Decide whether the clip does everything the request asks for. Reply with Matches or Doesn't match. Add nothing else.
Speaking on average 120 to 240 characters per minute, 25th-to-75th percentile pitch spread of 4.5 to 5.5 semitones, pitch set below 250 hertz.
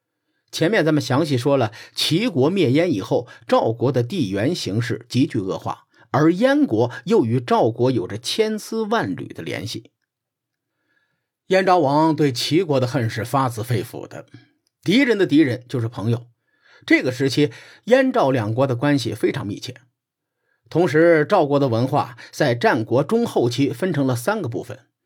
Matches